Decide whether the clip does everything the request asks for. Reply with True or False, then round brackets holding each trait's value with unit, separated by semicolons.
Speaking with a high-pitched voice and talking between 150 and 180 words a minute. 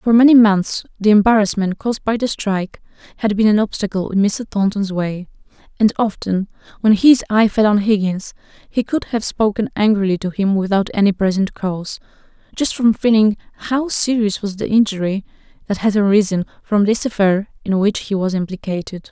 True (205 Hz; 175 wpm)